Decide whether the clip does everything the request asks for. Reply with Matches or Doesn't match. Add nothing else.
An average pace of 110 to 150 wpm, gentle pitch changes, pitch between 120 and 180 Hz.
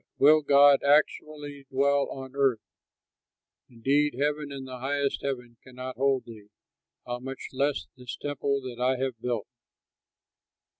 Matches